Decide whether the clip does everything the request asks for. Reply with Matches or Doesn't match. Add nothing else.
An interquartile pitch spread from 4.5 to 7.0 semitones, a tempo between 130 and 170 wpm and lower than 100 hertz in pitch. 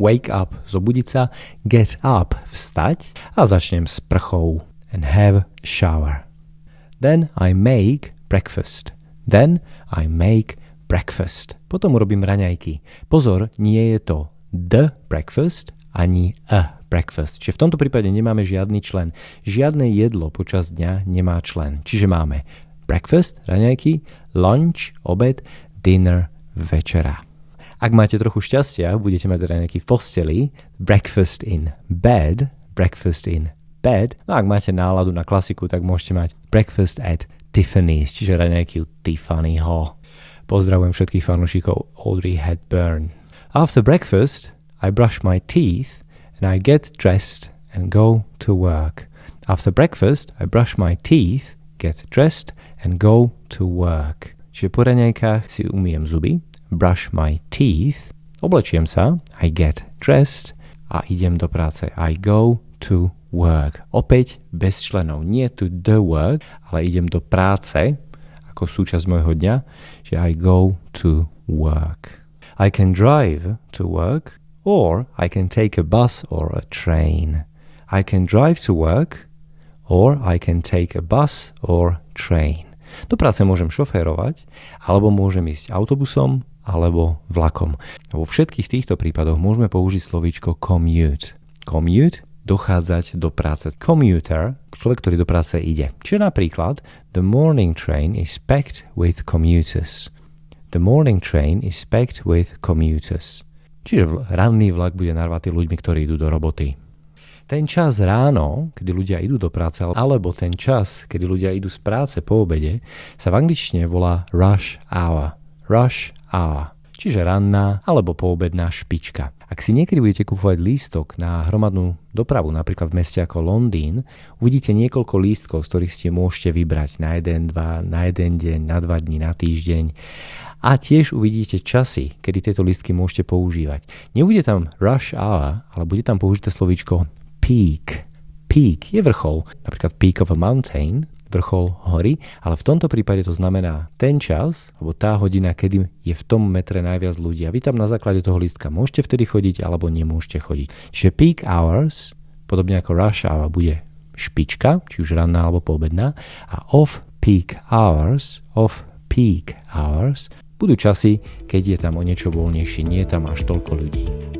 Matches